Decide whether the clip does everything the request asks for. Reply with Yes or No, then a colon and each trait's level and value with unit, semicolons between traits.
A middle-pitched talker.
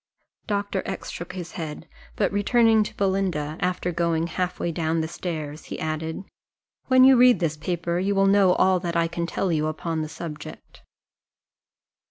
Yes: medium, 175 Hz